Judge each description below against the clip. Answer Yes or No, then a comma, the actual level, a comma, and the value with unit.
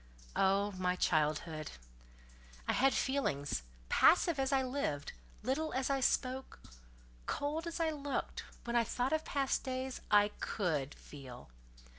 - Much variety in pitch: Yes, wide, 7.7 semitones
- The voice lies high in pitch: Yes, very high, 255 Hz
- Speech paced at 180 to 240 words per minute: No, slow, 135 wpm